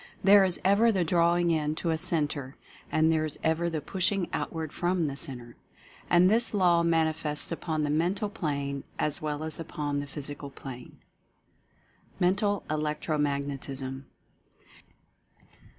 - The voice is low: No, medium, 160 Hz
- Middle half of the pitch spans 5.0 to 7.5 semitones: No, average, 3.2 semitones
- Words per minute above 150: No, average, 145 wpm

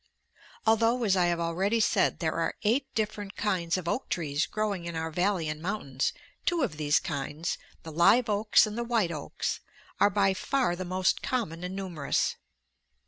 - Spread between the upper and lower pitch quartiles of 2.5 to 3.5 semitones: No, average, 4.4 semitones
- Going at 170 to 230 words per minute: Yes, average, 180 wpm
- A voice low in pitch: No, medium, 185 Hz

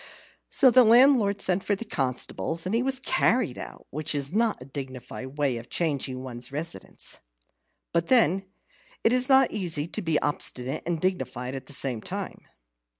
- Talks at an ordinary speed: Yes, average, 170 wpm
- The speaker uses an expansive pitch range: Yes, wide, 8.5 semitones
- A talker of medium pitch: Yes, medium, 165 Hz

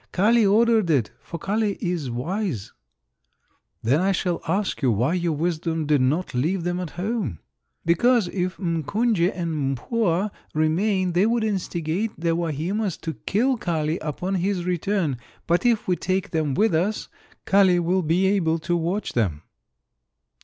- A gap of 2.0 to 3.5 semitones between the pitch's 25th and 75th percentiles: No, average, 3.9 semitones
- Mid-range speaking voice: Yes, medium, 175 Hz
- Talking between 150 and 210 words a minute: Yes, average, 155 wpm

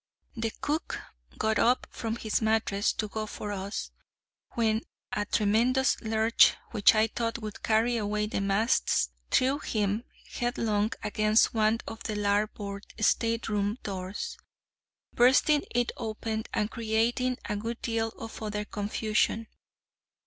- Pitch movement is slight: Yes, narrow, 1.7 semitones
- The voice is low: No, high, 220 Hz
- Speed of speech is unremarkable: No, slow, 130 wpm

